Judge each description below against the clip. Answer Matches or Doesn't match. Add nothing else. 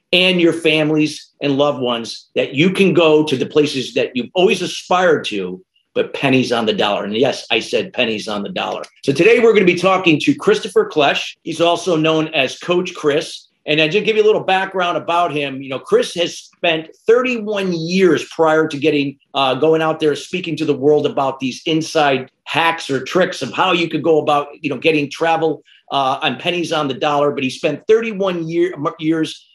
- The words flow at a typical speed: Doesn't match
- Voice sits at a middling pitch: Matches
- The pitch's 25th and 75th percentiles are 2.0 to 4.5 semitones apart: Matches